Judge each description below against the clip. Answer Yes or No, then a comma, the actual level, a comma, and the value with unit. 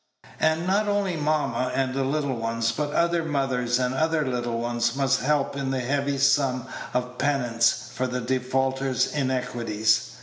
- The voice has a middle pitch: No, low, 130 Hz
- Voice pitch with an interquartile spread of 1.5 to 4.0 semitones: Yes, average, 2.7 semitones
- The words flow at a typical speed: Yes, average, 160 wpm